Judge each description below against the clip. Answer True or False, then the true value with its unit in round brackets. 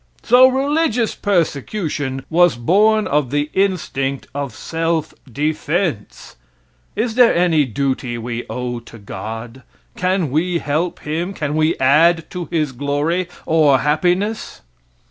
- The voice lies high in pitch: False (155 Hz)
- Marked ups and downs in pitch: False (4.9 semitones)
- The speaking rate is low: True (125 wpm)